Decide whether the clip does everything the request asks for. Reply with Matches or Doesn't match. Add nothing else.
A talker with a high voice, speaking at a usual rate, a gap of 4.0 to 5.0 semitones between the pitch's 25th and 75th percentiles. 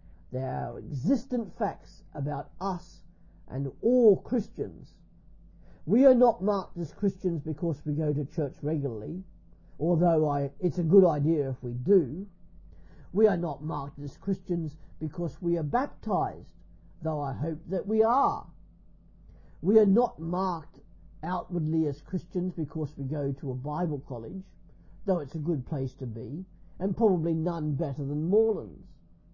Doesn't match